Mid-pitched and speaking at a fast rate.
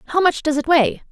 No: very high, 315 Hz; fast, 270 wpm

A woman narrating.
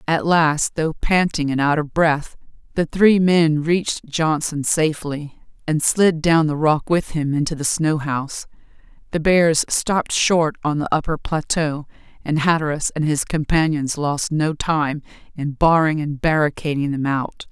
Yes: female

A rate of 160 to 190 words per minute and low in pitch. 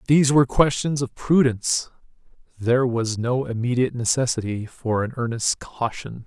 No: slow, 135 wpm; low, 125 Hz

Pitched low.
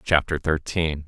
Yes: very low, 75 Hz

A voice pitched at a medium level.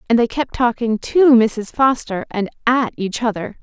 No: high, 235 Hz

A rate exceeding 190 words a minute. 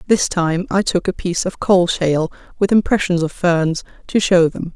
Yes: average, 200 wpm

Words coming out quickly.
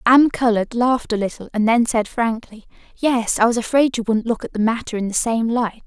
Yes: fast, 235 wpm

